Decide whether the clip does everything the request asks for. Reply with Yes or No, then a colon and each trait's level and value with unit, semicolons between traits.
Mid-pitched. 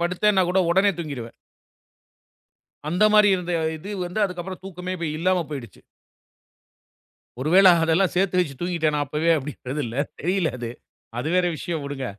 Yes: medium, 175 Hz